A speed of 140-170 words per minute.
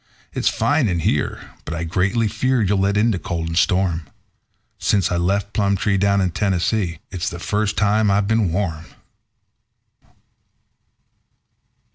Yes: average, 145 wpm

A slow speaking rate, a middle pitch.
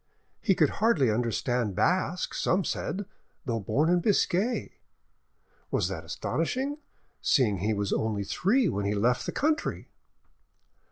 Yes: slow, 130 wpm; medium, 145 Hz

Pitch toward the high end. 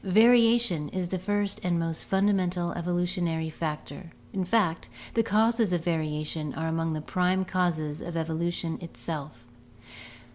No: medium, 175 Hz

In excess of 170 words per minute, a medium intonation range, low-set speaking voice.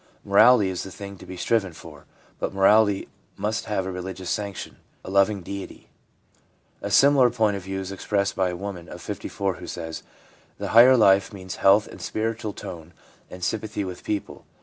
No: average, 180 wpm; narrow, 2.3 semitones; low, 100 Hz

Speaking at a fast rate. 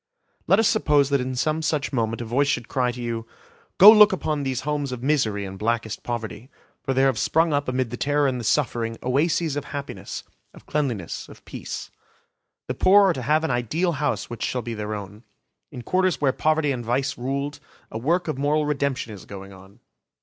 Yes: fast, 210 wpm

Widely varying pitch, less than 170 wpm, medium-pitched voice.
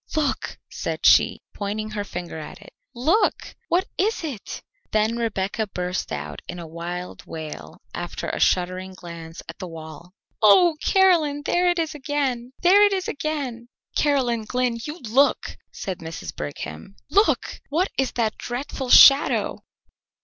No: wide, 8.6 semitones; average, 150 wpm; high, 235 Hz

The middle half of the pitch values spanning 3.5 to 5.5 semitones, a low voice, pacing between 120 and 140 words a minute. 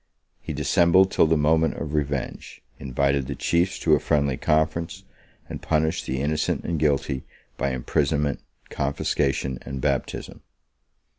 No: narrow, 2.5 semitones; very low, 75 Hz; slow, 135 wpm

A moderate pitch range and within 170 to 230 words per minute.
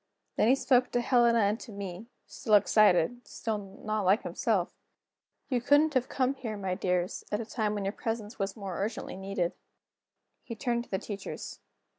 Yes: average, 3.6 semitones; average, 180 wpm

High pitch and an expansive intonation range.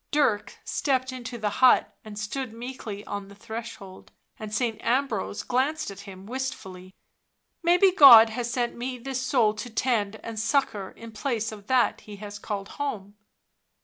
No: high, 230 Hz; average, 3.9 semitones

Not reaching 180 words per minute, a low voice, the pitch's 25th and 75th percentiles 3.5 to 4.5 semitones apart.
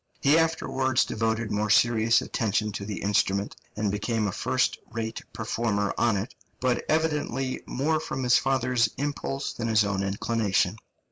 Yes: average, 150 wpm; low, 115 Hz; average, 4.1 semitones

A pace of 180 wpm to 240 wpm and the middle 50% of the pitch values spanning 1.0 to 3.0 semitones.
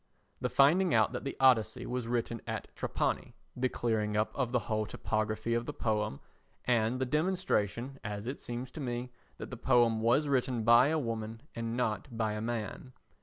Yes: average, 185 wpm; average, 2.7 semitones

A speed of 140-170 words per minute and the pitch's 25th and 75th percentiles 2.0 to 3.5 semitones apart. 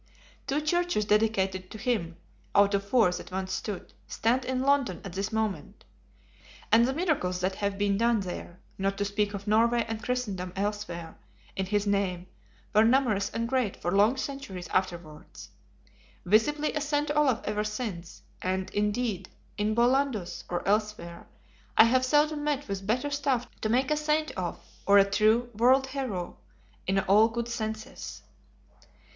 No: average, 160 wpm; average, 4.6 semitones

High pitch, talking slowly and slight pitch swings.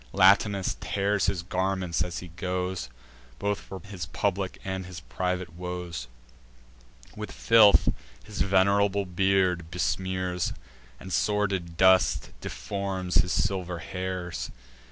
No: very low, 95 Hz; slow, 115 wpm; narrow, 1.6 semitones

